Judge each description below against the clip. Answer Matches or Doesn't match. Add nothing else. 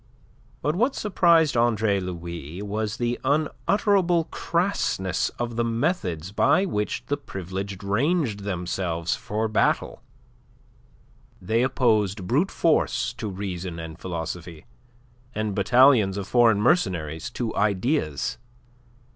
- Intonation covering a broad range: Matches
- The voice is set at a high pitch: Doesn't match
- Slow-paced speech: Matches